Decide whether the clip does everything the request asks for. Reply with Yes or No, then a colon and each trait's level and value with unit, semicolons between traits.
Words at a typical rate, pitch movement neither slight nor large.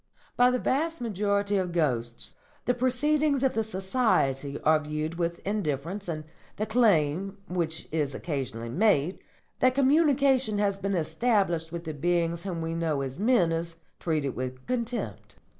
No: average, 150 wpm; wide, 6.9 semitones